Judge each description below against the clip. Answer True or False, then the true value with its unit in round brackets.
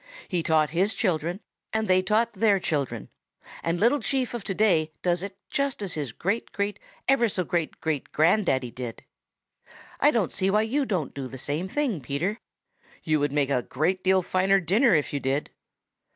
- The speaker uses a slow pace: False (185 wpm)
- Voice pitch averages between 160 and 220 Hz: True (185 Hz)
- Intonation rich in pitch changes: True (5.7 semitones)